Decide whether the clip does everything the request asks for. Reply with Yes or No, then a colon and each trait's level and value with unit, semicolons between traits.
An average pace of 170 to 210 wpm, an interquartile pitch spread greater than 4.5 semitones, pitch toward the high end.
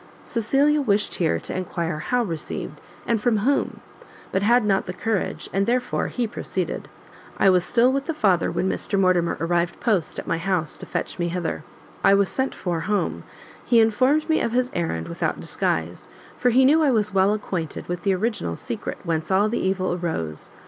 Yes: average, 190 wpm; wide, 5.4 semitones; high, 195 Hz